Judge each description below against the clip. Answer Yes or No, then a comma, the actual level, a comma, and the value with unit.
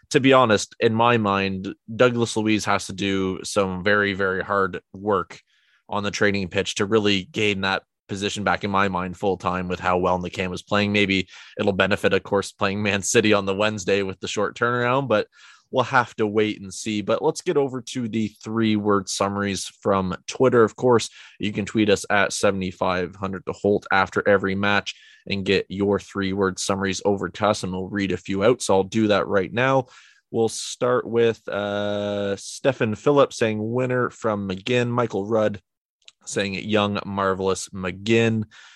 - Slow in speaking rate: No, average, 185 wpm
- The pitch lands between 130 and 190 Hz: No, low, 100 Hz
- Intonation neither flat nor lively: No, narrow, 2.3 semitones